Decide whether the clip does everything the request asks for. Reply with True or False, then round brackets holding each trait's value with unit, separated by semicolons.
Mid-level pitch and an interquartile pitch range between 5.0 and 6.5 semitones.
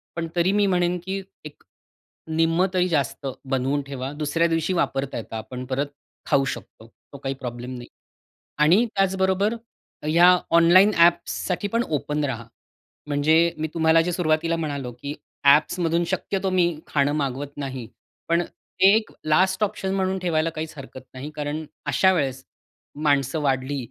False (155 Hz; 4.3 semitones)